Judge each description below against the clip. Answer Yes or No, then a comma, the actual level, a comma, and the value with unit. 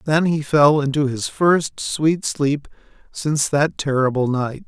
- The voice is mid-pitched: Yes, medium, 145 Hz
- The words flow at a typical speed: Yes, average, 155 wpm